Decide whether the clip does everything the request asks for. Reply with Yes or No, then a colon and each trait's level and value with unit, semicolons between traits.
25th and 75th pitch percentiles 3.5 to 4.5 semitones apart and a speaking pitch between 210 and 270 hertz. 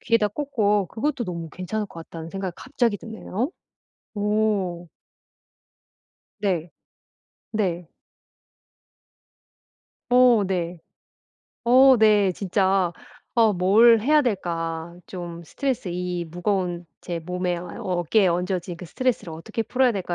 No: average, 4.1 semitones; high, 190 Hz